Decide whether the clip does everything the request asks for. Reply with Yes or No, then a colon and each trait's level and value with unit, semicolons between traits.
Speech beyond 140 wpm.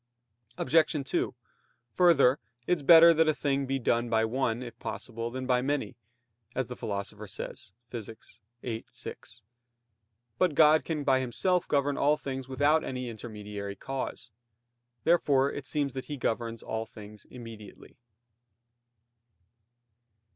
No: slow, 135 wpm